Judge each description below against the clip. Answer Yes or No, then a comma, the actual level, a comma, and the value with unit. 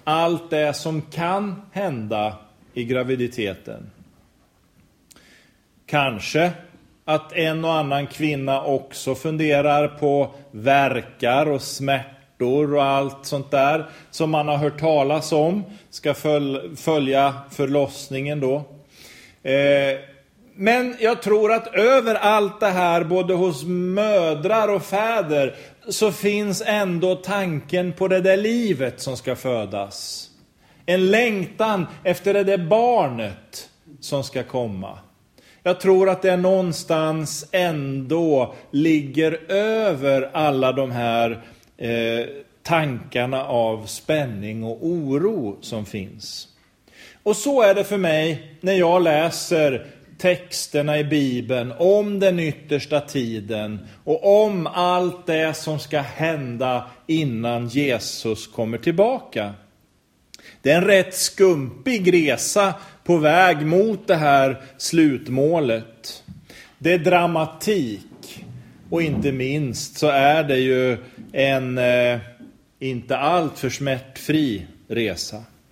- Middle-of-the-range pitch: Yes, medium, 150 Hz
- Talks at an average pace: No, slow, 110 wpm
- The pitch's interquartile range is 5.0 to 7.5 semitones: Yes, average, 5.3 semitones